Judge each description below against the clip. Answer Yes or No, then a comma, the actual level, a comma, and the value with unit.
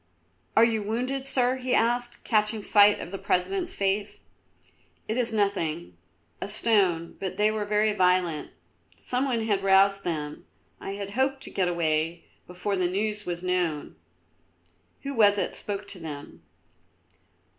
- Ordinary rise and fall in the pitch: Yes, average, 3.8 semitones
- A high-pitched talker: Yes, high, 205 Hz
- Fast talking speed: No, average, 150 wpm